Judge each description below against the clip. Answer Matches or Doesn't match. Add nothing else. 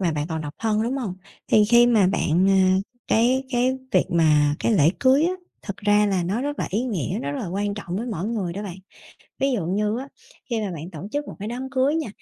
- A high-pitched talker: Matches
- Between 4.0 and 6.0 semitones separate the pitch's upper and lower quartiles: Matches